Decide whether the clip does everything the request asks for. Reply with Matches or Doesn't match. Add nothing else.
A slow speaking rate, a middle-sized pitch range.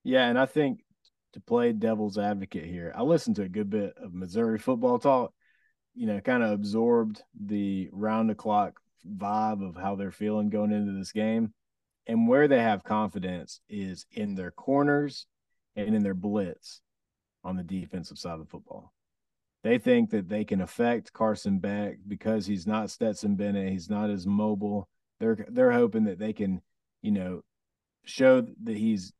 Doesn't match